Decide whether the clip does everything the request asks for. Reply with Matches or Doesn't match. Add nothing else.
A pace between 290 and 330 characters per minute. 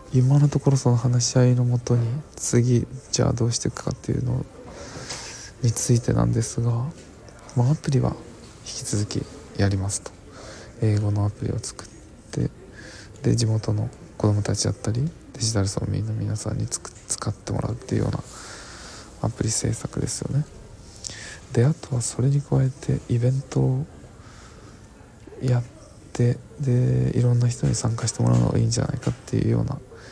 Matches